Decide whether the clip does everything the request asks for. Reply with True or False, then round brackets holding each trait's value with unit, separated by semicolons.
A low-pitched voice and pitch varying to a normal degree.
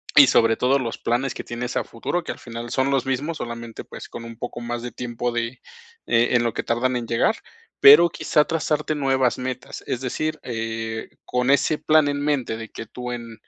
True (125 Hz; 3.0 semitones)